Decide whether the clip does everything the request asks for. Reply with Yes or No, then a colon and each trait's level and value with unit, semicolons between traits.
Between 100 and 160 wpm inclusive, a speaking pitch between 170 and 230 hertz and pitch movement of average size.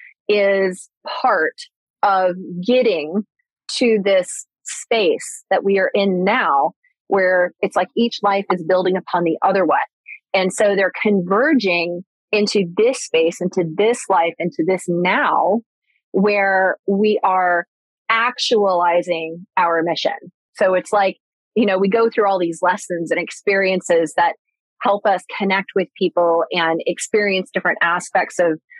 Yes: average, 140 wpm; high, 190 Hz; average, 3.0 semitones